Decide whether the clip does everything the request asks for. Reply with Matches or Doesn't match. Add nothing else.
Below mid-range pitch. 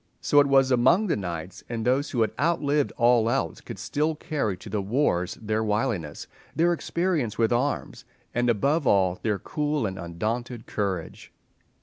Matches